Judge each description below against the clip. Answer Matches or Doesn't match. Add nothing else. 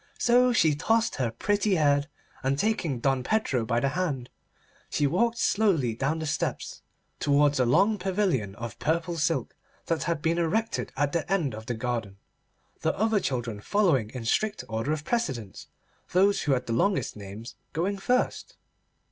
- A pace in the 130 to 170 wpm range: Matches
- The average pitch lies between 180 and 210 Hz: Doesn't match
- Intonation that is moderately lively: Doesn't match